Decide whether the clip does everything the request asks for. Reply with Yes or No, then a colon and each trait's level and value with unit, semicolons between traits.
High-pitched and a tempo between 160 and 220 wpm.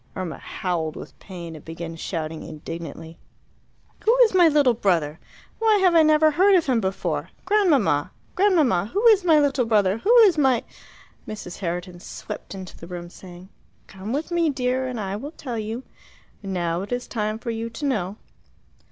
Yes: high, 220 Hz; average, 180 wpm